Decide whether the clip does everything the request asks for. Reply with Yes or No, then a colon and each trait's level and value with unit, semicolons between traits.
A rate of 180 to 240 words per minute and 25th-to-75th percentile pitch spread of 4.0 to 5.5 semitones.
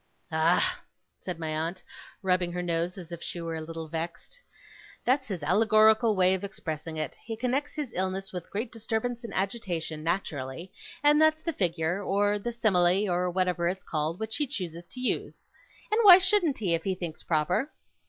Yes: average, 185 wpm; average, 5.2 semitones